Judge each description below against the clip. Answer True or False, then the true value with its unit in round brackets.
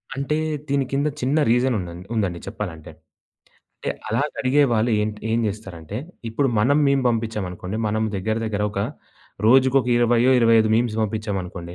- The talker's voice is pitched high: False (110 Hz)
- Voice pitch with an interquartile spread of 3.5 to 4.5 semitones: True (3.9 semitones)